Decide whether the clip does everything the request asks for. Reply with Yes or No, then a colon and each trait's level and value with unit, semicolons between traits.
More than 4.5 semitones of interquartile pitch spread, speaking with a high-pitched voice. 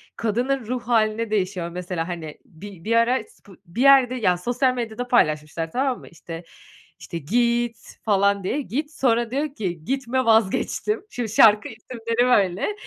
Yes: average, 5.2 semitones; high, 225 Hz